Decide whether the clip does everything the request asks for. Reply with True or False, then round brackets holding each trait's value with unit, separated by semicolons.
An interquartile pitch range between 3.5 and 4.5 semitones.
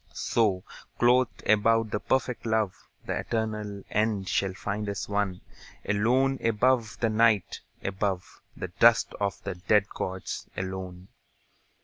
False (2.9 semitones)